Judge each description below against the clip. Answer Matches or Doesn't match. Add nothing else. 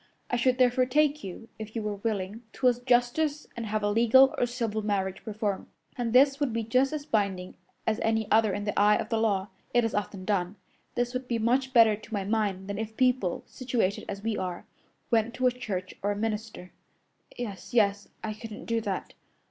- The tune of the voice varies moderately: Matches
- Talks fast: Matches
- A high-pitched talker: Matches